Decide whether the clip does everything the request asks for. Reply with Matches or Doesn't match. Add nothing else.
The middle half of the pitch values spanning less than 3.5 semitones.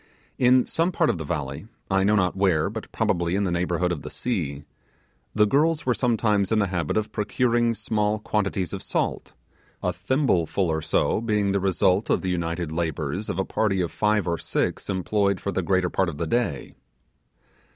Doesn't match